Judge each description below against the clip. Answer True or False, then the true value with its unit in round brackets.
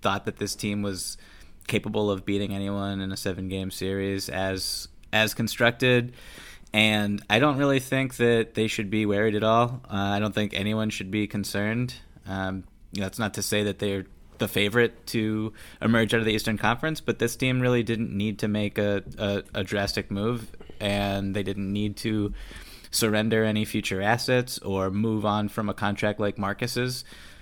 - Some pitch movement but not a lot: False (2.1 semitones)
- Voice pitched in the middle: False (105 Hz)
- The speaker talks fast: False (185 wpm)